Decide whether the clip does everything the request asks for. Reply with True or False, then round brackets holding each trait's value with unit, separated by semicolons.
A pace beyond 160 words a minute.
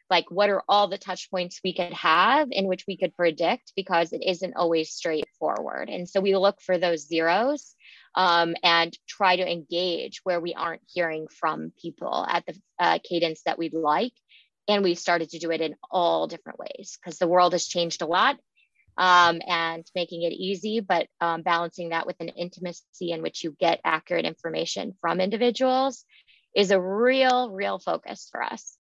True (185 wpm)